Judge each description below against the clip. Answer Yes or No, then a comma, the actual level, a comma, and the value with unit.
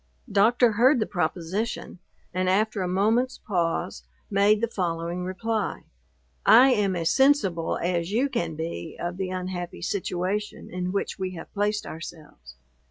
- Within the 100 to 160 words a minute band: Yes, average, 145 wpm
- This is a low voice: No, medium, 185 Hz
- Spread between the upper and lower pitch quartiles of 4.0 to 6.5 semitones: No, average, 3.6 semitones